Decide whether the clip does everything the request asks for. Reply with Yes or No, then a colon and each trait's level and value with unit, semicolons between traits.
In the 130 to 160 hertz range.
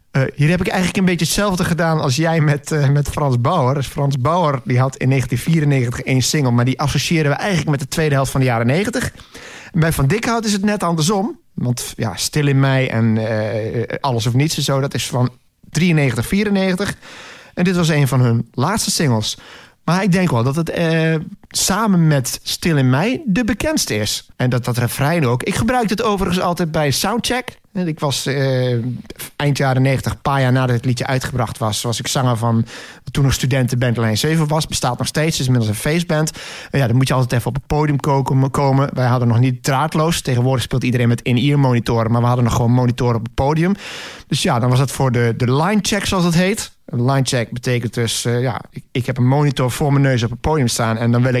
Yes: low, 135 Hz